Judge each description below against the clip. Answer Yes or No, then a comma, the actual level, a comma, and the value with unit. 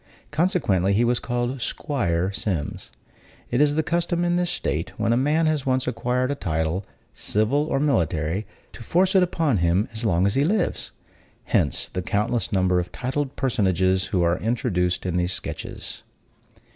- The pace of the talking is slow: No, average, 170 wpm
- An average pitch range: No, wide, 7.9 semitones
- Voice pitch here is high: No, low, 115 Hz